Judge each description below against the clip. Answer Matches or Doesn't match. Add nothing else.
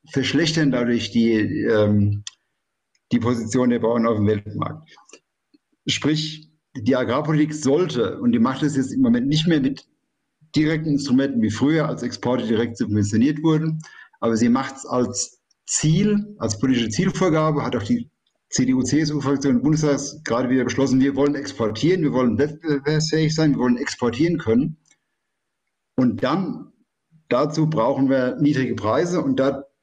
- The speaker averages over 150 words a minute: Doesn't match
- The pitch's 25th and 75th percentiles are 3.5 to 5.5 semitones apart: Matches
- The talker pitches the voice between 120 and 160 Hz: Matches